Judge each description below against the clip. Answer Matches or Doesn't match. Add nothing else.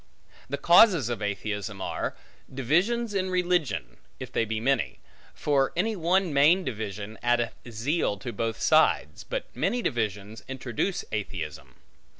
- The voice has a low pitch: Matches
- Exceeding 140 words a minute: Doesn't match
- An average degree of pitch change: Doesn't match